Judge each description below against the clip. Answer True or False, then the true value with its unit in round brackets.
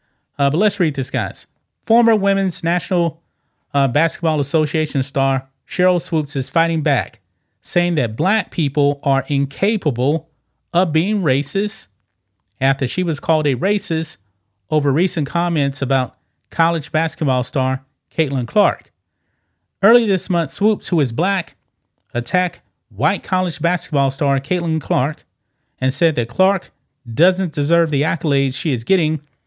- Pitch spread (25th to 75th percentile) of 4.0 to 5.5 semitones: True (4.5 semitones)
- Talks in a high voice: False (155 Hz)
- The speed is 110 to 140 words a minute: True (135 wpm)